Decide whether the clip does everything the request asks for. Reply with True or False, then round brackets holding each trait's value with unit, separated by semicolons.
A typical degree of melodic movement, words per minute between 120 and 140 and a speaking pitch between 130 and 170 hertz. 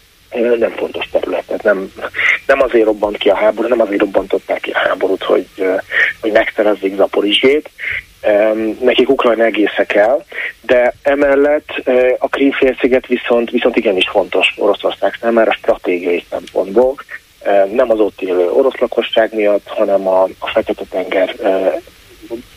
False (3.7 semitones; 130 wpm; 115 Hz)